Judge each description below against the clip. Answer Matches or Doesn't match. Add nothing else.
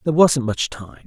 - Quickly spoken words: Matches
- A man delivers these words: Matches